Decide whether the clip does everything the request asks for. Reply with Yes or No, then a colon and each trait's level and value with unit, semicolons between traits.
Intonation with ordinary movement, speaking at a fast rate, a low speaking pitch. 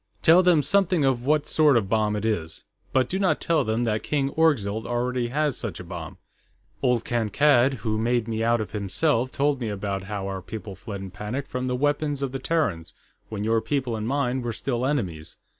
Yes: average, 4.8 semitones; fast, 210 wpm; low, 120 Hz